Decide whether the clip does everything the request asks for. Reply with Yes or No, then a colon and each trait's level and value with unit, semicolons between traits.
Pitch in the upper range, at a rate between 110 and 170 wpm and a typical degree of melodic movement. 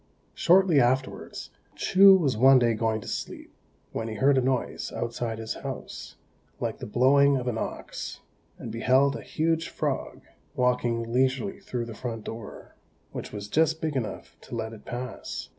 No: low, 125 Hz; average, 165 wpm; average, 3.6 semitones